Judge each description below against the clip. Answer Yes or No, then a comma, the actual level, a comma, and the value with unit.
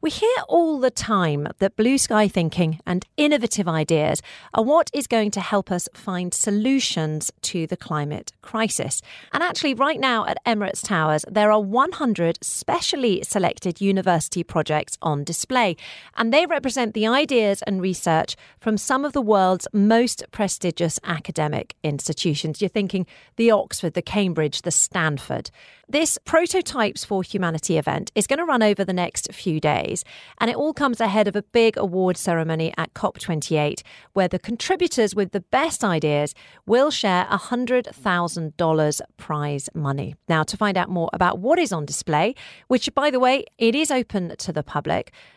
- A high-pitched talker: Yes, high, 195 Hz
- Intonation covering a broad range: Yes, wide, 6.3 semitones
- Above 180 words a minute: No, average, 165 wpm